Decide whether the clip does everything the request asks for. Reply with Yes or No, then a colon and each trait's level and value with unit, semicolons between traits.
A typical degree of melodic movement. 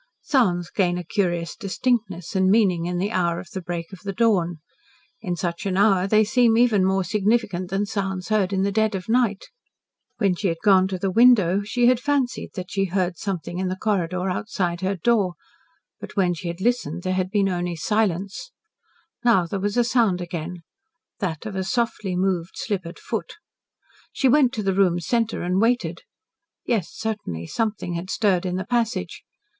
Yes: average, 3.4 semitones